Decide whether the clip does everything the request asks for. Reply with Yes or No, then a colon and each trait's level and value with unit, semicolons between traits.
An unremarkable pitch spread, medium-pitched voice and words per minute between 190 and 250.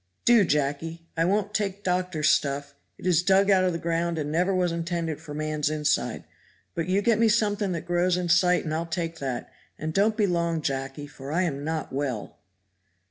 Yes: average, 3.4 semitones; medium, 170 Hz; average, 200 wpm